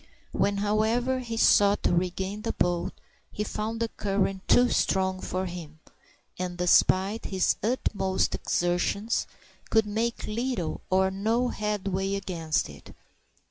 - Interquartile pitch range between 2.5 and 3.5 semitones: Yes, average, 3.0 semitones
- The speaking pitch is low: No, high, 200 Hz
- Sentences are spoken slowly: Yes, slow, 130 wpm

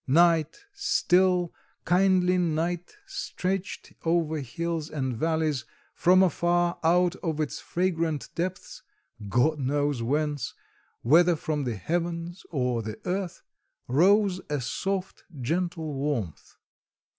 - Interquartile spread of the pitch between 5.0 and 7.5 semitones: No, average, 3.5 semitones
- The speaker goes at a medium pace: No, slow, 110 wpm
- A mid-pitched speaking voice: Yes, medium, 165 Hz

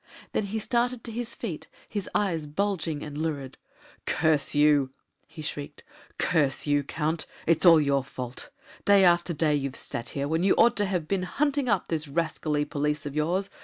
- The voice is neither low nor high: Yes, medium, 160 Hz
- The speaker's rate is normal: Yes, average, 180 wpm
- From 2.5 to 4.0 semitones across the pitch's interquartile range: No, average, 4.9 semitones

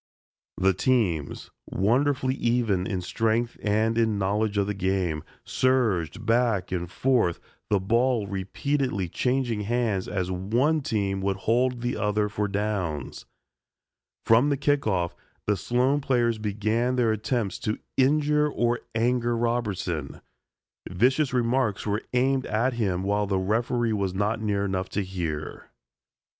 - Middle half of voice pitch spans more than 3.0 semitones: Yes, average, 4.1 semitones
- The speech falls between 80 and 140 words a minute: Yes, slow, 135 wpm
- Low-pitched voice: Yes, low, 110 Hz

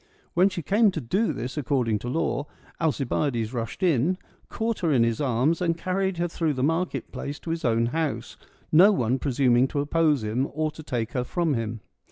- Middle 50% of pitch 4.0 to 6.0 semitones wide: Yes, wide, 5.5 semitones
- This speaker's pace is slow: No, average, 200 wpm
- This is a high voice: No, medium, 145 Hz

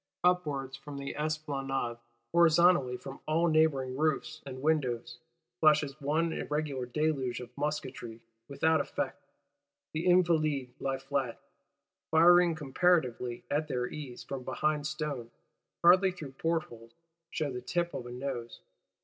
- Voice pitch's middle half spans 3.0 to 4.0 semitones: Yes, average, 3.6 semitones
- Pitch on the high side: No, medium, 145 Hz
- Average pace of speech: No, slow, 125 wpm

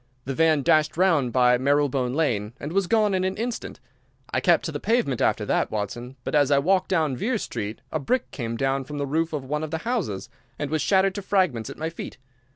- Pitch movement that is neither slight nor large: No, wide, 6.1 semitones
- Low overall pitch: No, medium, 150 Hz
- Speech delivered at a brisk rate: Yes, fast, 230 wpm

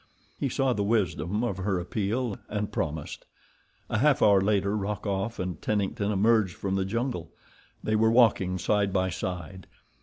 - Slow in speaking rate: No, average, 155 wpm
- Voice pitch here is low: Yes, low, 100 Hz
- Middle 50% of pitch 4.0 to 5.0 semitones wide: No, average, 3.0 semitones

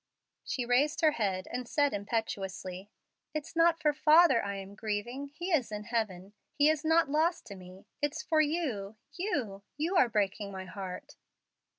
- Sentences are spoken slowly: No, average, 170 wpm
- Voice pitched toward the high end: Yes, high, 240 Hz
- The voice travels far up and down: Yes, wide, 7.4 semitones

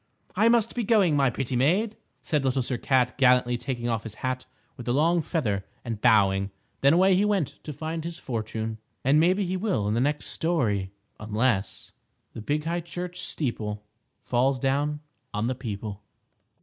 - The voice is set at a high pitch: No, low, 135 Hz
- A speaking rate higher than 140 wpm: Yes, average, 175 wpm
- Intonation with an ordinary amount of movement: No, wide, 6.5 semitones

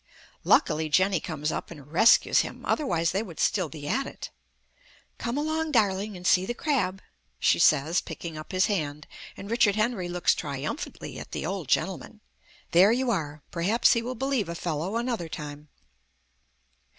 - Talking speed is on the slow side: No, average, 165 wpm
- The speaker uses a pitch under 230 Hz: Yes, medium, 185 Hz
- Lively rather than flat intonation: Yes, wide, 6.5 semitones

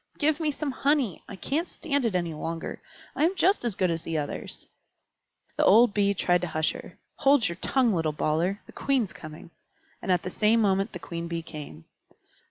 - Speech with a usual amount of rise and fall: No, wide, 8.0 semitones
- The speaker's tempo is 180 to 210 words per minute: Yes, average, 200 wpm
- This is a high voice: Yes, high, 195 Hz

